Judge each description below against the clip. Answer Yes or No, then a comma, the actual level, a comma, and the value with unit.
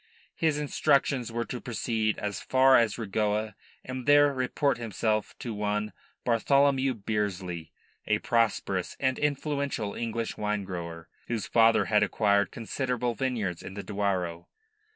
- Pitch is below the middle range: Yes, low, 115 Hz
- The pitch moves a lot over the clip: No, average, 4.0 semitones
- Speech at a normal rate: No, slow, 130 wpm